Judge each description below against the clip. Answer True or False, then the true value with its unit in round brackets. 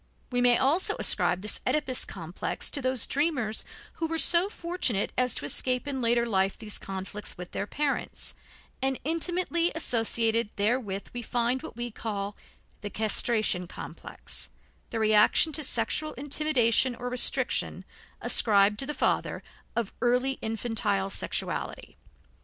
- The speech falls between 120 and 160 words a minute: True (140 wpm)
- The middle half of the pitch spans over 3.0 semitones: True (4.3 semitones)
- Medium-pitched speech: False (240 Hz)